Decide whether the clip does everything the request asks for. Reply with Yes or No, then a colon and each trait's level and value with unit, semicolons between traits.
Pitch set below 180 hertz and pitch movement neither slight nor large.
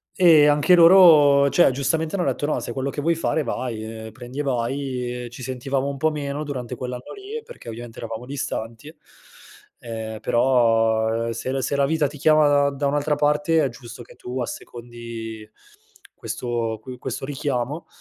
Yes: low, 135 Hz; average, 3.7 semitones